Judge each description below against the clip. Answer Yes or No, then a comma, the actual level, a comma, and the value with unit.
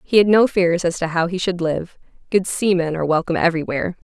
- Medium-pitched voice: Yes, medium, 175 Hz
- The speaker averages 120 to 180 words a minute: No, fast, 205 wpm